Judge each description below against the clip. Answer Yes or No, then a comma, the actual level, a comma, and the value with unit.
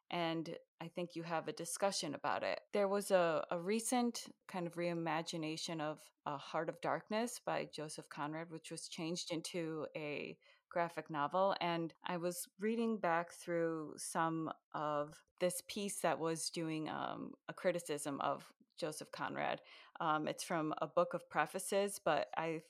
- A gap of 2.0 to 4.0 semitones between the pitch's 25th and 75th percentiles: Yes, narrow, 2.6 semitones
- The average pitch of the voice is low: No, medium, 170 Hz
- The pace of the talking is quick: No, average, 160 wpm